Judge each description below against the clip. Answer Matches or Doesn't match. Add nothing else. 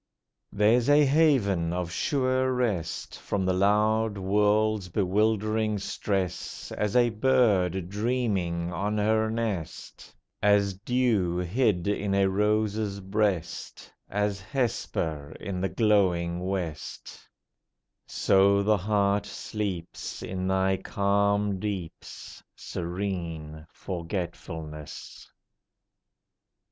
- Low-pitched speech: Matches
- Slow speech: Matches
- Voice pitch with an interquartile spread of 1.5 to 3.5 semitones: Matches